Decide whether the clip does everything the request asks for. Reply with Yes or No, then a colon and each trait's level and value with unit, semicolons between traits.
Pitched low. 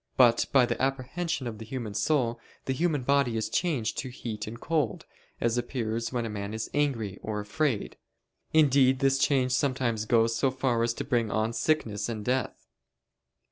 Yes: low, 120 Hz